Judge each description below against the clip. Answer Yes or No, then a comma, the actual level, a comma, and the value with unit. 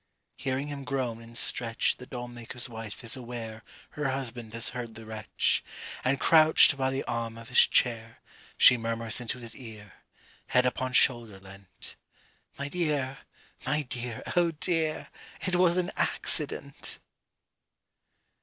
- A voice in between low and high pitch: No, low, 125 Hz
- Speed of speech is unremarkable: Yes, average, 145 wpm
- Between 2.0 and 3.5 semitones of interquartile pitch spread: Yes, average, 3.1 semitones